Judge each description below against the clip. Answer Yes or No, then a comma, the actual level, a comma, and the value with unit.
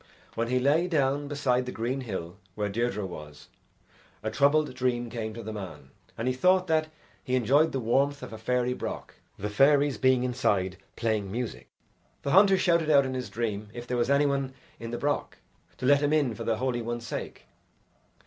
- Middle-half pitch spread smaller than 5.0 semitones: Yes, average, 4.0 semitones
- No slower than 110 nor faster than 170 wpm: No, average, 195 wpm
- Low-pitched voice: Yes, low, 125 Hz